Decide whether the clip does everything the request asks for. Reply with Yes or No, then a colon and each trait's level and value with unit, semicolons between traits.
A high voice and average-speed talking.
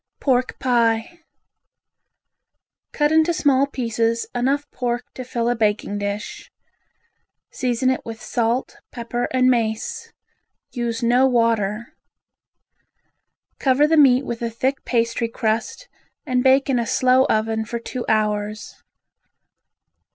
No: high, 240 Hz; slow, 120 wpm